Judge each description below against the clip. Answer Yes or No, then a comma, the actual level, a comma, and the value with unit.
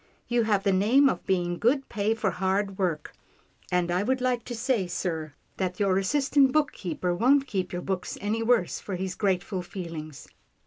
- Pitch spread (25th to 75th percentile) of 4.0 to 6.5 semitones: Yes, average, 4.8 semitones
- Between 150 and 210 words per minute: Yes, average, 180 wpm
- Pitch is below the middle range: No, high, 195 Hz